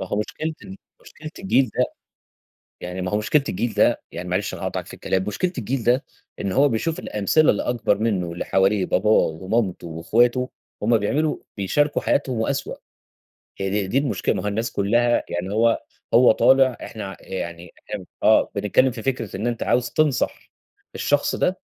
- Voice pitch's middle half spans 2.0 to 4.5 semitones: No, average, 4.9 semitones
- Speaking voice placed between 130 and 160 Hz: No, low, 110 Hz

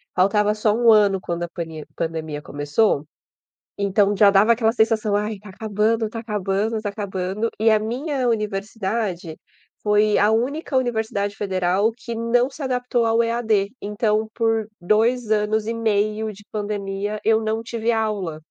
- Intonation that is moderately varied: No, narrow, 2.2 semitones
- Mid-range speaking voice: No, high, 215 Hz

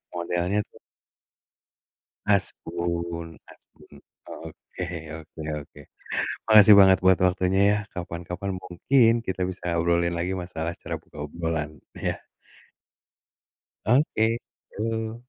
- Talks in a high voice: No, very low, 90 Hz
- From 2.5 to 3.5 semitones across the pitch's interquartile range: Yes, average, 2.8 semitones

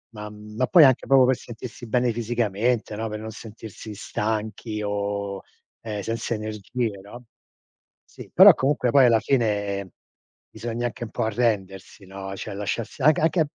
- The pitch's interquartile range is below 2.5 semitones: No, average, 2.8 semitones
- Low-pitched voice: Yes, low, 110 Hz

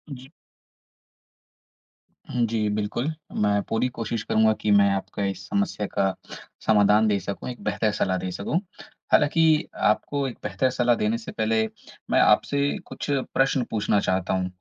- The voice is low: Yes, low, 110 Hz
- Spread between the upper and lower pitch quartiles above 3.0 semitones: Yes, average, 3.6 semitones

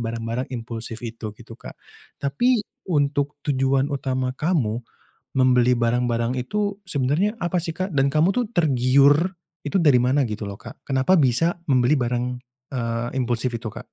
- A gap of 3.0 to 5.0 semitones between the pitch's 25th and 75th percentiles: Yes, average, 3.9 semitones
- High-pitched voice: No, low, 130 Hz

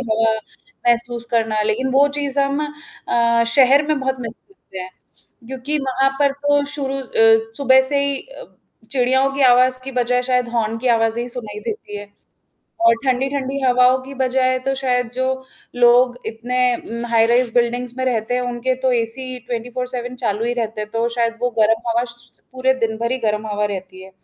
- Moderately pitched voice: No, high, 245 Hz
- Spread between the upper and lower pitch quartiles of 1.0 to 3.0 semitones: Yes, narrow, 2.4 semitones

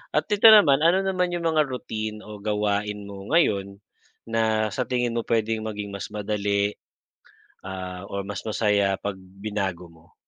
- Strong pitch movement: No, average, 3.5 semitones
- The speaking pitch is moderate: No, low, 105 Hz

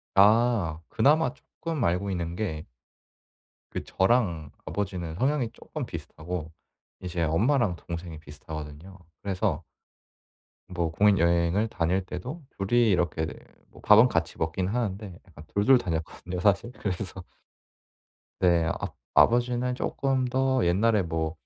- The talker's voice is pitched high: No, very low, 95 Hz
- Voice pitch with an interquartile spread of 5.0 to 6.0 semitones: Yes, wide, 5.4 semitones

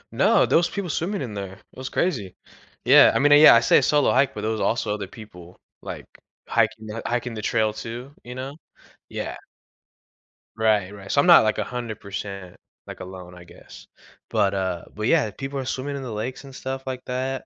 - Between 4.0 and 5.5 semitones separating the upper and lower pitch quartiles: Yes, average, 4.3 semitones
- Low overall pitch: Yes, low, 115 Hz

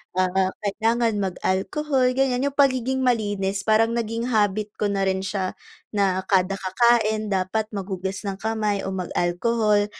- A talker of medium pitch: No, high, 210 Hz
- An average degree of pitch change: Yes, average, 3.4 semitones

